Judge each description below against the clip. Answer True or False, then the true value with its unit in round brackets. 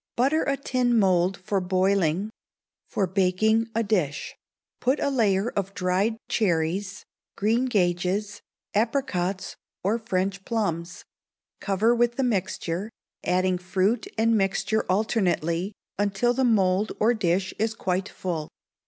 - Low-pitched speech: False (195 Hz)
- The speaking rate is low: True (120 wpm)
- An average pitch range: True (3.6 semitones)